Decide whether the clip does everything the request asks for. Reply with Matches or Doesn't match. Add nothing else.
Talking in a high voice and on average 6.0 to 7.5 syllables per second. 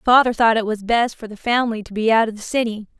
Matches